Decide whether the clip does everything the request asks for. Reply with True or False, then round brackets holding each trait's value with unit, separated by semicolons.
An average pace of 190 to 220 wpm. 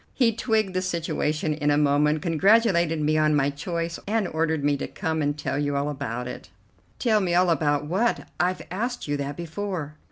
True (195 wpm)